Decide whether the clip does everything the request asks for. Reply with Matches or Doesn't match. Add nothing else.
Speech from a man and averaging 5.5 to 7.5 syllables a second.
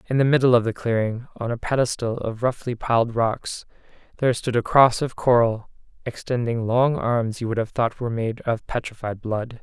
Doesn't match